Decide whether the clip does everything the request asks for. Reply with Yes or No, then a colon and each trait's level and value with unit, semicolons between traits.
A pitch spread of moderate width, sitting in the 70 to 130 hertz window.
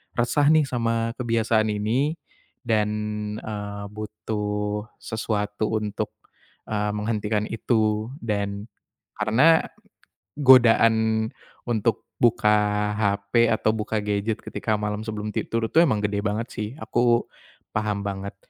No: narrow, 1.8 semitones; low, 110 Hz